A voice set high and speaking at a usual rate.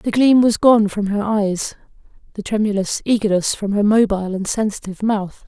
Yes: high, 210 Hz; average, 175 wpm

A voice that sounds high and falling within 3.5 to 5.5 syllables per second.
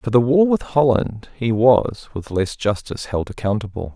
No: low, 115 Hz; 4.7 syllables/s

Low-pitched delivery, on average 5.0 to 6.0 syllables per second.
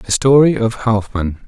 No: low, 115 Hz; 4.3 syllables/s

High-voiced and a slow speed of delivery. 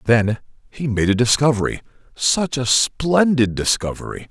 No: low, 125 Hz; slow, 125 wpm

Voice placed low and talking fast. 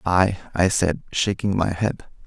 No: very low, 95 Hz; average, 160 wpm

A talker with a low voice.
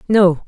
No: medium, 185 Hz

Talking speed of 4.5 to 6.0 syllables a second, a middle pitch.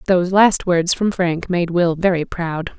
No: 4.2 syllables/s; medium, 175 Hz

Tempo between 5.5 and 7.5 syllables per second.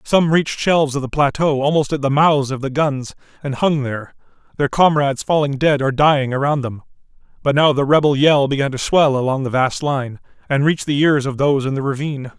Yes: 5.8 syllables/s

